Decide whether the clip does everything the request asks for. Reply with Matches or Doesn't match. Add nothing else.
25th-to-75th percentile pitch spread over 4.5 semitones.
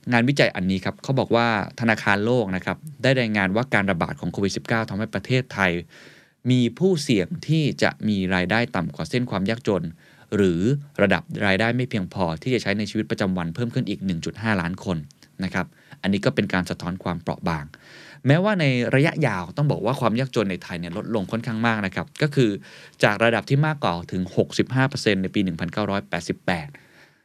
Matches